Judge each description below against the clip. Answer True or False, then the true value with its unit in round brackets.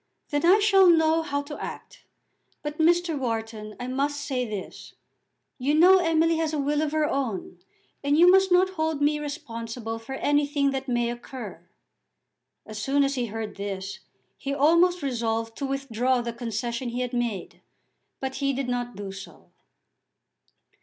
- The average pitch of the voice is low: False (275 Hz)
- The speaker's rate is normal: True (165 wpm)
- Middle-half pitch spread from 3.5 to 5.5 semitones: True (4.7 semitones)